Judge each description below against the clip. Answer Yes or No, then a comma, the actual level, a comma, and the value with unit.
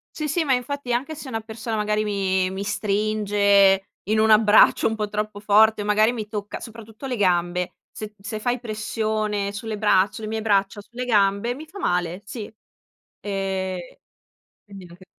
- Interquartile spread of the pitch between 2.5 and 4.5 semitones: No, narrow, 2.0 semitones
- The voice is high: Yes, high, 210 Hz